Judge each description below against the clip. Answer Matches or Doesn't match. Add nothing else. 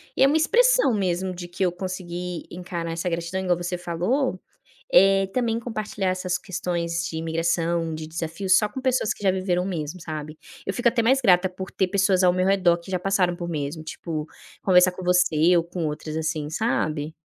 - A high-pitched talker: Doesn't match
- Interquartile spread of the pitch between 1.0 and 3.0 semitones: Matches